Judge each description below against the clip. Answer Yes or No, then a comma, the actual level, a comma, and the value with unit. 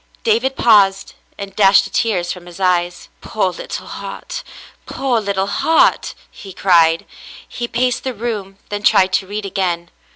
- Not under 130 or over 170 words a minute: Yes, average, 155 wpm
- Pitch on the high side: Yes, high, 195 Hz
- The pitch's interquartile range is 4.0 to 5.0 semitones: No, average, 3.4 semitones